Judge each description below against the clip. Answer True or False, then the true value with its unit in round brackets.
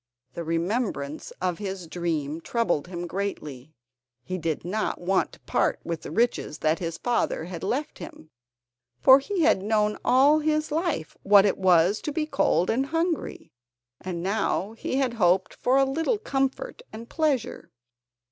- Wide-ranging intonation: True (7.8 semitones)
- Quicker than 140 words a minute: True (160 wpm)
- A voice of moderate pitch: False (200 Hz)